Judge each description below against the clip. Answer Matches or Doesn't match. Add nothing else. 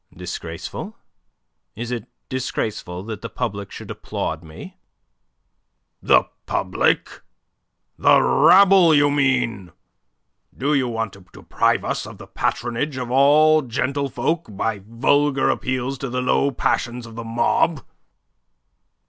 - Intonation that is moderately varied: Matches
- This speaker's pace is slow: Matches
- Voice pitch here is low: Matches